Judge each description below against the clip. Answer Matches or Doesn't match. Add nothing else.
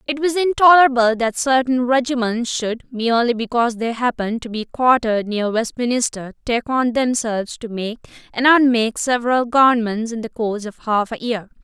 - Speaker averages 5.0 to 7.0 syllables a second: Matches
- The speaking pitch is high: Matches